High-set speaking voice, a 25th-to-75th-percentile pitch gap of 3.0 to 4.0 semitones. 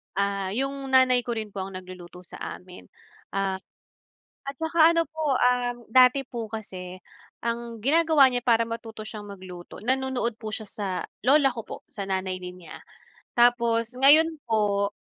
No: high, 230 Hz; average, 4.8 semitones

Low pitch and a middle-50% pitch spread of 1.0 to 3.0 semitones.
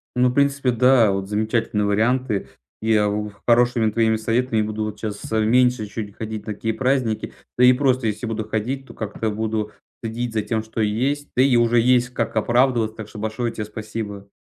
Yes: low, 110 Hz; narrow, 2.5 semitones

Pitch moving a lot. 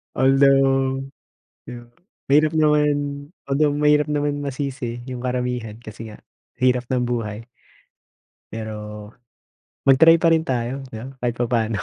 No: average, 3.4 semitones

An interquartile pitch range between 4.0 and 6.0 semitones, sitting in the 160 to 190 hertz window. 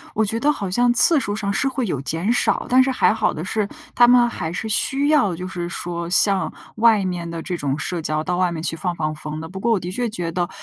Yes: wide, 5.4 semitones; medium, 185 Hz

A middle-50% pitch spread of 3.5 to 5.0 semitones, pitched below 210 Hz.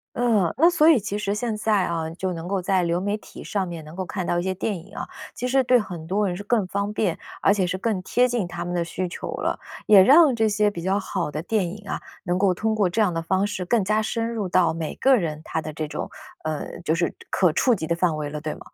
Yes: average, 3.8 semitones; high, 190 Hz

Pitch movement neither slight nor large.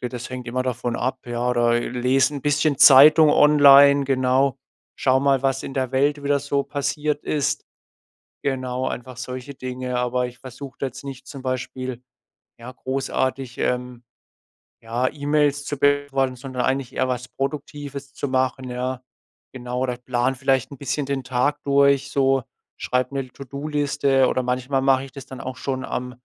No: narrow, 1.8 semitones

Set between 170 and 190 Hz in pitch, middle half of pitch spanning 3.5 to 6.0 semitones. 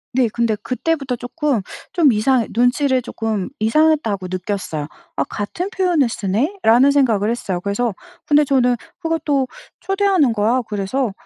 No: high, 245 Hz; wide, 5.4 semitones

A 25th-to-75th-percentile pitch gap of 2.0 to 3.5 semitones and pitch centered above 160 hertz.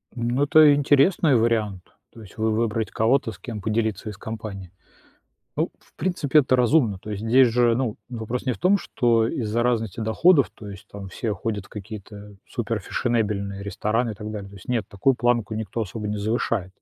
No: average, 2.8 semitones; low, 110 Hz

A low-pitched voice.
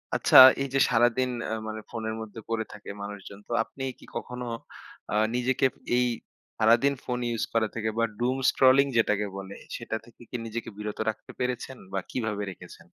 Yes: low, 115 Hz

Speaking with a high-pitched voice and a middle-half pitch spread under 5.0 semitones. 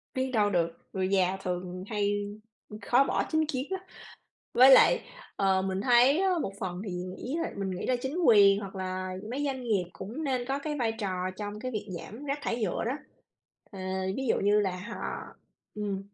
No: high, 210 Hz; wide, 5.4 semitones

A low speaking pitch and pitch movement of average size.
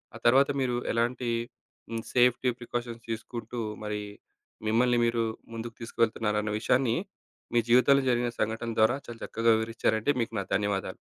No: low, 115 Hz; narrow, 1.5 semitones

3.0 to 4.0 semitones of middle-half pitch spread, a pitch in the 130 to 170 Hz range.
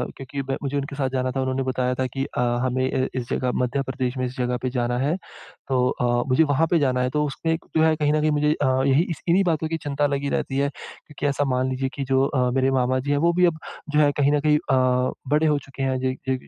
No: narrow, 2.4 semitones; low, 135 Hz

